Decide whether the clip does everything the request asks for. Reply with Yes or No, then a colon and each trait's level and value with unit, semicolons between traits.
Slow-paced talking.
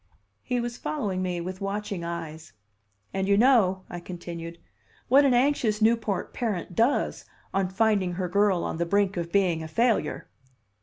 No: average, 160 wpm